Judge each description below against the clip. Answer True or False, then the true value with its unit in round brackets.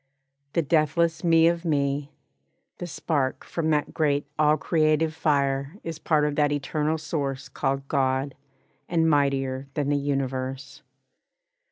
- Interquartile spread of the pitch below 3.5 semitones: True (2.5 semitones)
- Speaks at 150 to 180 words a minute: False (135 wpm)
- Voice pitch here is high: False (145 Hz)